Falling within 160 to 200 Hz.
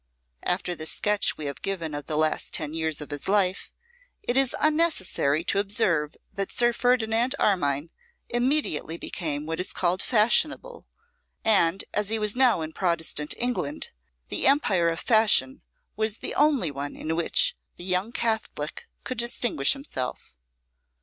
Yes: high, 190 Hz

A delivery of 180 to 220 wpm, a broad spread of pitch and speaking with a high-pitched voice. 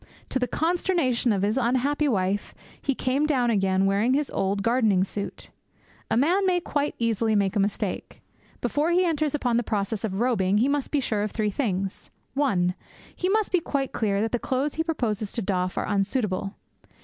Yes: average, 190 wpm; wide, 6.2 semitones; high, 235 Hz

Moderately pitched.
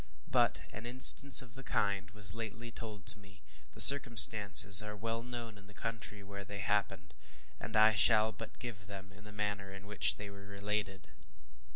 No: low, 105 Hz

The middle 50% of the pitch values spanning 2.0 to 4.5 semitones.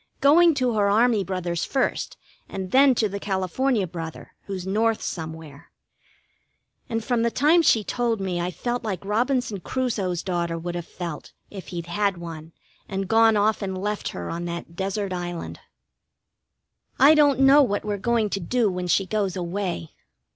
No: average, 4.9 semitones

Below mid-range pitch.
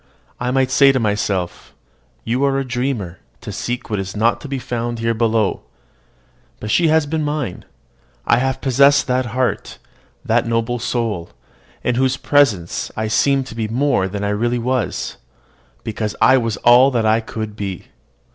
Yes: low, 120 Hz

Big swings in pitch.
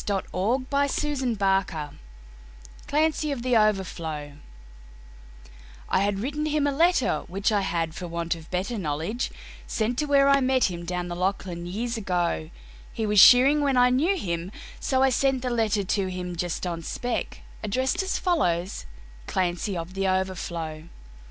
Yes: wide, 6.9 semitones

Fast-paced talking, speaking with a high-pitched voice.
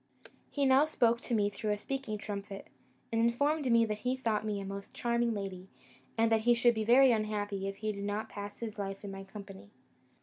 Yes: fast, 210 wpm; high, 215 Hz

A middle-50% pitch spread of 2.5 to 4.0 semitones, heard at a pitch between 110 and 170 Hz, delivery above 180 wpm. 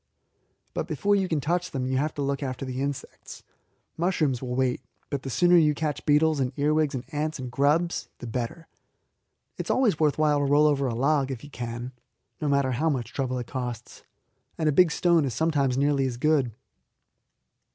Yes: average, 3.1 semitones; medium, 140 Hz; average, 200 wpm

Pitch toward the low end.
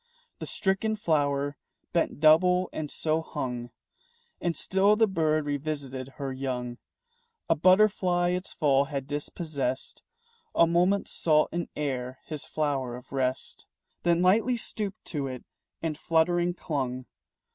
No: medium, 155 Hz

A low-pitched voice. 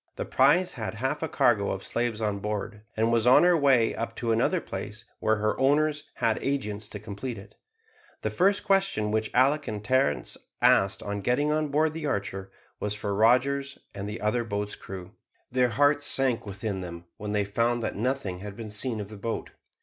Yes: low, 115 Hz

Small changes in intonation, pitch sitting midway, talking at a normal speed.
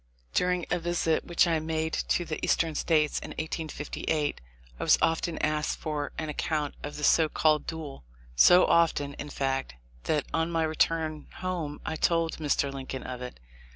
Yes: narrow, 2.0 semitones; medium, 155 Hz; average, 170 wpm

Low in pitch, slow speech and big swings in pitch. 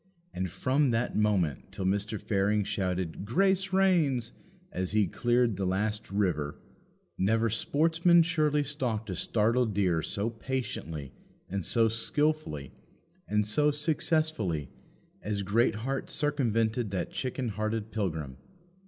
Yes: low, 110 Hz; slow, 120 wpm; wide, 5.7 semitones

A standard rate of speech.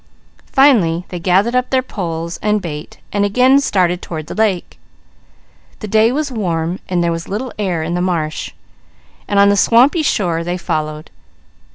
Yes: average, 170 wpm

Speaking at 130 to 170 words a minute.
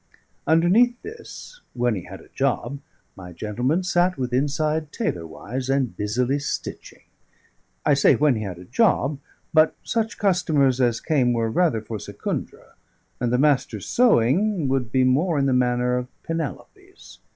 Yes: average, 150 wpm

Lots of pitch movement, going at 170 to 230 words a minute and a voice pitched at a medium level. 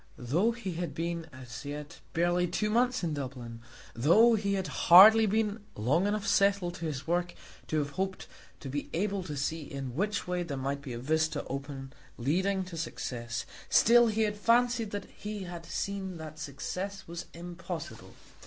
Yes: wide, 5.7 semitones; average, 175 wpm; medium, 175 Hz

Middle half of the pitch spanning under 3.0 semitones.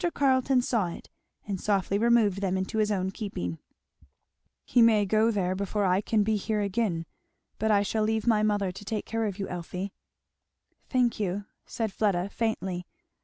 Yes: narrow, 2.6 semitones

